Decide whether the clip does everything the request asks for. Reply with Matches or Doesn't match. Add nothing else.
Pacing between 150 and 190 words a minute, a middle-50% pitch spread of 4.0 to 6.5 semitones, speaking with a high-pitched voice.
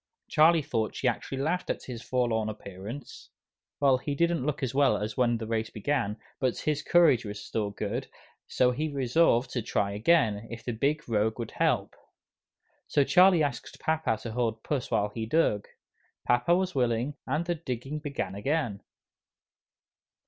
Doesn't match